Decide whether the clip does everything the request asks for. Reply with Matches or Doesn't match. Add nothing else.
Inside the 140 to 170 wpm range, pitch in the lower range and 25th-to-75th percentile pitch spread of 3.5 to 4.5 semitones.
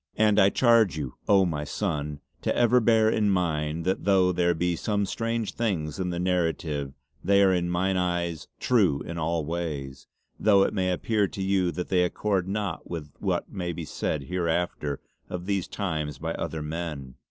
Doesn't match